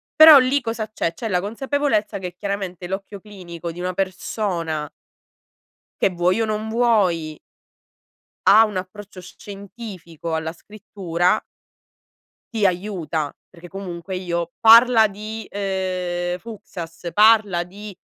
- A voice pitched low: No, high, 195 Hz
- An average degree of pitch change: Yes, average, 3.5 semitones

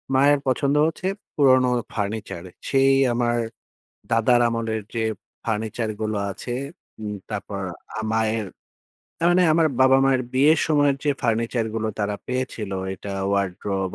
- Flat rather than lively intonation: No, average, 3.9 semitones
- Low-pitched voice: Yes, low, 115 Hz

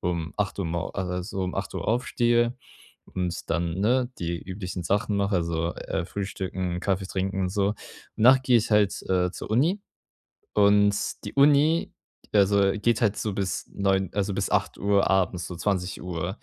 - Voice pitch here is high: No, low, 100 Hz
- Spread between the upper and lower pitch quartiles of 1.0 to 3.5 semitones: Yes, average, 2.7 semitones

